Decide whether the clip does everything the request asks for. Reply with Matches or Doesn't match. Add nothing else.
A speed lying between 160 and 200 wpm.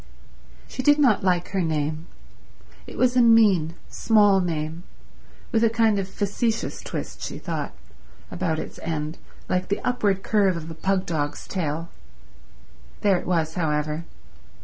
Doesn't match